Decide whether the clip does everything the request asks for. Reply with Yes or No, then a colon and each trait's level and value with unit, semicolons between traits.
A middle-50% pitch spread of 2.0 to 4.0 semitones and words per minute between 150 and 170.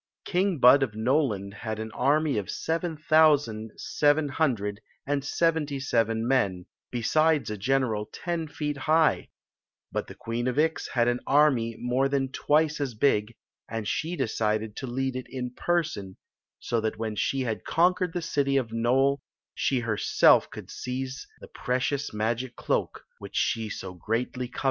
No: average, 4.7 semitones; average, 165 wpm